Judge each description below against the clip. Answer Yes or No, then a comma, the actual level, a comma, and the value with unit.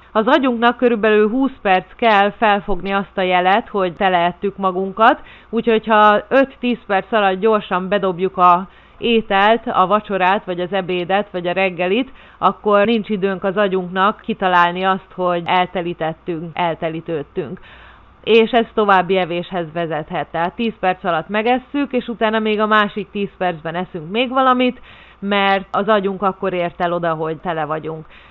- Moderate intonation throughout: Yes, average, 3.2 semitones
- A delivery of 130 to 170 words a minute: Yes, average, 150 wpm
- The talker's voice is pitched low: No, high, 195 Hz